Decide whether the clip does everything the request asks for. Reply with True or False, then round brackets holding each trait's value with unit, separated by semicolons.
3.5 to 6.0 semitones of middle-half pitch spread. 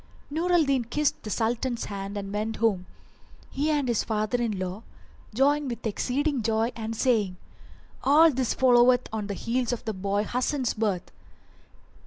True (3.8 semitones)